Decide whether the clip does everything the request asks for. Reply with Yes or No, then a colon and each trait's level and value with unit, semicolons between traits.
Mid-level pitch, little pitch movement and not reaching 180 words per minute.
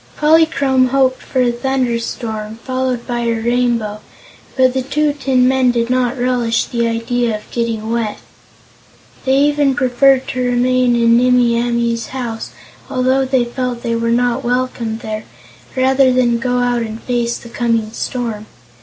No: high, 245 Hz; narrow, 1.7 semitones; average, 155 wpm